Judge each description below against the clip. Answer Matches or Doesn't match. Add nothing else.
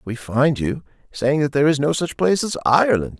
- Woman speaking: Doesn't match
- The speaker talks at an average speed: Doesn't match